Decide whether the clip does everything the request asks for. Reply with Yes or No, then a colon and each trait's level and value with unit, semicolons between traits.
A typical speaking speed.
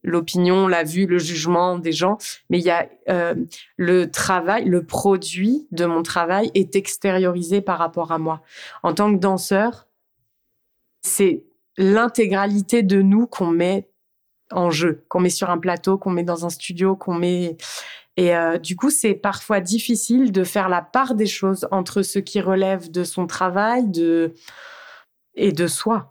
Yes: average, 170 wpm